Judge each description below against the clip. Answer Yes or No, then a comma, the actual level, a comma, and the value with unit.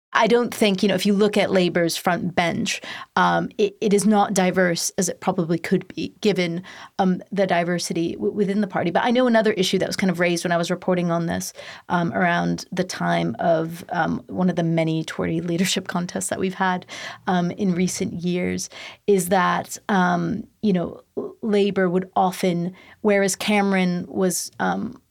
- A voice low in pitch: No, medium, 185 Hz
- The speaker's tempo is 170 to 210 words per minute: Yes, average, 190 wpm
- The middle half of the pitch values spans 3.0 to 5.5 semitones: No, narrow, 2.5 semitones